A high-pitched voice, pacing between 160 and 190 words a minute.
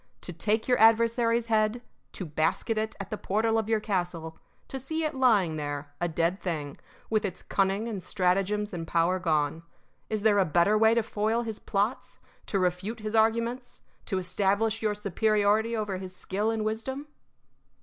Yes: high, 210 Hz; average, 175 wpm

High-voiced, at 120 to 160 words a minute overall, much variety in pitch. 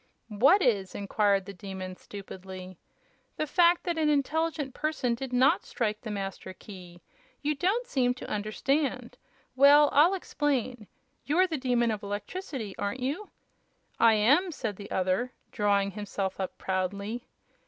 Yes: high, 235 Hz; average, 145 wpm; wide, 6.6 semitones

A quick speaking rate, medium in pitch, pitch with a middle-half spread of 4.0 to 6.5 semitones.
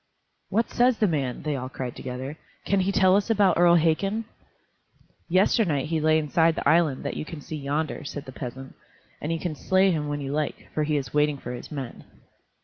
Yes: fast, 210 wpm; medium, 155 Hz; average, 4.4 semitones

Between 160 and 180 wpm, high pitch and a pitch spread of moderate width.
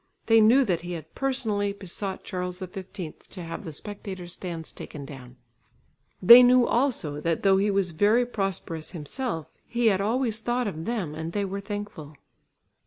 Yes: average, 170 wpm; high, 195 Hz; average, 4.9 semitones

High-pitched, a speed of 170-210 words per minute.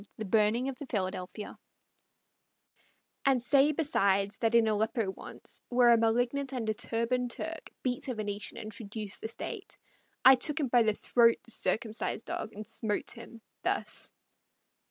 No: high, 230 Hz; average, 155 wpm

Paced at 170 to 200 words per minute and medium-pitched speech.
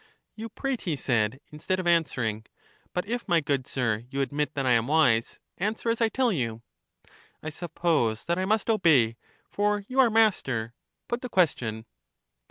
Yes: average, 175 wpm; medium, 160 Hz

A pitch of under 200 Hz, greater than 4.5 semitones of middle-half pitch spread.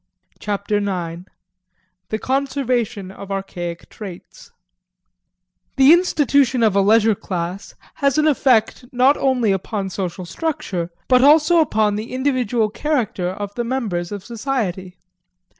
No: high, 215 Hz; wide, 5.6 semitones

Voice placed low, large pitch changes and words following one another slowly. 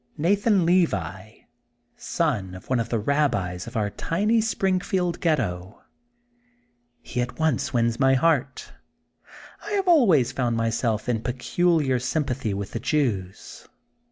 Yes: low, 130 Hz; wide, 6.8 semitones; slow, 130 wpm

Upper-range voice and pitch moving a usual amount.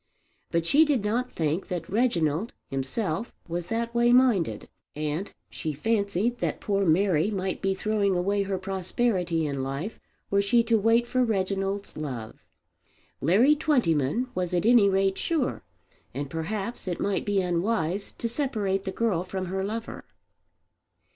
Yes: high, 195 Hz; average, 4.9 semitones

